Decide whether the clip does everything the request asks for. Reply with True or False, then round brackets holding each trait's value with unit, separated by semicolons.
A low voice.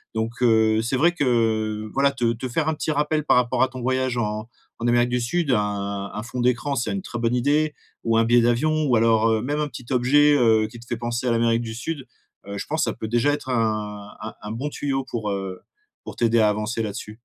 True (120 Hz)